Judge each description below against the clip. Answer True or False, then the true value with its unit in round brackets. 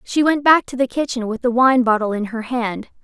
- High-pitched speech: True (245 Hz)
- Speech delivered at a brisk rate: True (255 wpm)